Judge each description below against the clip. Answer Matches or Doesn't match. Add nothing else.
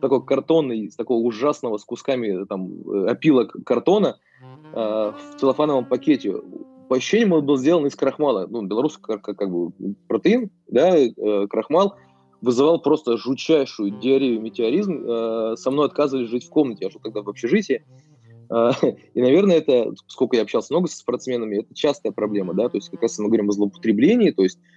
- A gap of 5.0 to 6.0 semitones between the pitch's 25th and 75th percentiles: Matches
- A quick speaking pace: Matches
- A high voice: Doesn't match